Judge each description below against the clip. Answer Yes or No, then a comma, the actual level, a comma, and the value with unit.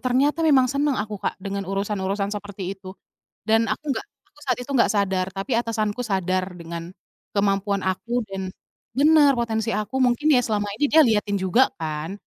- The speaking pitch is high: Yes, high, 210 Hz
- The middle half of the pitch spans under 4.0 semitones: No, average, 4.3 semitones